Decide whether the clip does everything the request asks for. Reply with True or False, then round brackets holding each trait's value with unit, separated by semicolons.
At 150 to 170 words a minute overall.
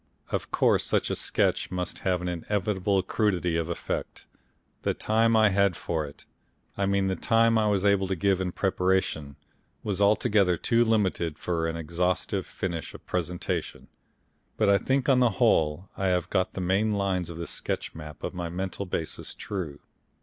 False (180 wpm)